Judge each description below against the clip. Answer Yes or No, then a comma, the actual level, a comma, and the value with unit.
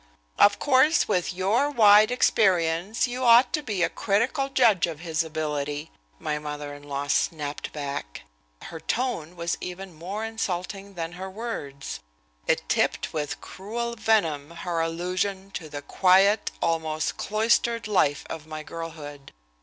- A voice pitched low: No, medium, 180 Hz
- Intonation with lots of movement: Yes, wide, 5.7 semitones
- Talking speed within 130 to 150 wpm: Yes, average, 145 wpm